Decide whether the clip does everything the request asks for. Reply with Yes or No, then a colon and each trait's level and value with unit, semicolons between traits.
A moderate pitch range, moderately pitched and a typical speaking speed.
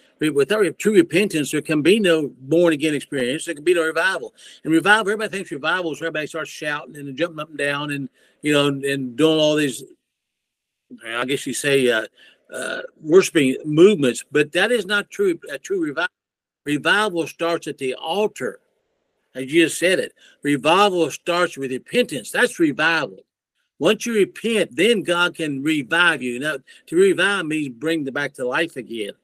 No: wide, 6.2 semitones; medium, 160 Hz; average, 175 wpm